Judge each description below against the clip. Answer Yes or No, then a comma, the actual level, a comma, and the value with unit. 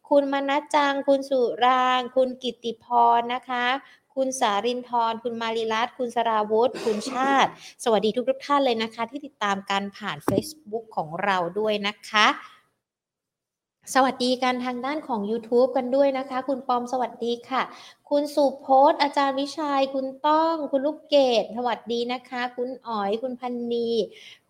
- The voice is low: No, very high, 250 Hz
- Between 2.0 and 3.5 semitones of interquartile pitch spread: Yes, average, 2.9 semitones